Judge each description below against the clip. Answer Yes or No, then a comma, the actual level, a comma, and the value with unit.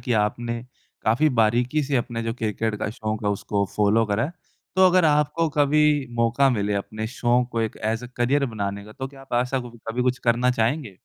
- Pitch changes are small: No, average, 3.6 semitones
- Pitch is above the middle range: No, low, 120 Hz